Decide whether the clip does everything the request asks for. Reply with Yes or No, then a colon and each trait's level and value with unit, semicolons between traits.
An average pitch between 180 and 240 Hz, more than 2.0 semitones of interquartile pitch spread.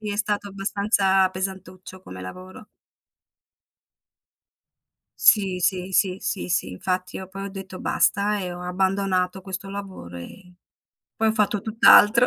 No: high, 190 Hz; narrow, 1.7 semitones